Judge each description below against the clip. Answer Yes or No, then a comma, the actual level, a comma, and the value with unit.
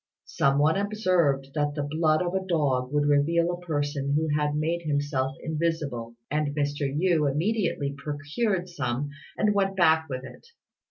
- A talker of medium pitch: Yes, medium, 150 Hz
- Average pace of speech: Yes, average, 160 wpm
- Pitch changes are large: No, average, 3.1 semitones